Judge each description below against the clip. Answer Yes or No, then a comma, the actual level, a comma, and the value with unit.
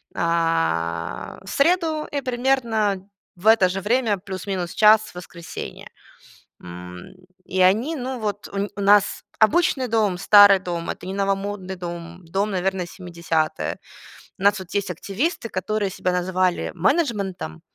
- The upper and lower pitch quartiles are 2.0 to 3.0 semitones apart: No, average, 3.5 semitones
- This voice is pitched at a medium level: No, high, 195 Hz